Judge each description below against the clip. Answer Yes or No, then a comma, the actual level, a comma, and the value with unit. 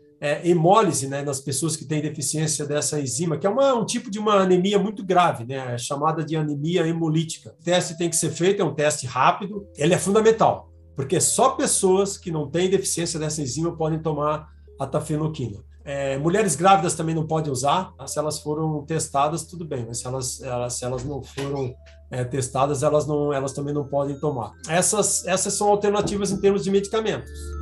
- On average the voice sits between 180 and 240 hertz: No, medium, 155 Hz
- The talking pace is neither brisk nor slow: No, fast, 195 wpm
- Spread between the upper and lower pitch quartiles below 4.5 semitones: No, average, 4.8 semitones